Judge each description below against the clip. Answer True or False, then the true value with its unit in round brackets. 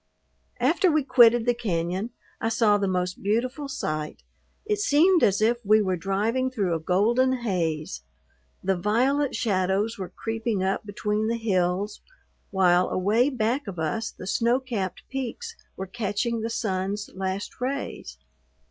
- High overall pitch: True (215 Hz)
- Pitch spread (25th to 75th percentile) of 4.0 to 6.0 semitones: True (4.3 semitones)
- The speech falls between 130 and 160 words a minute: True (150 wpm)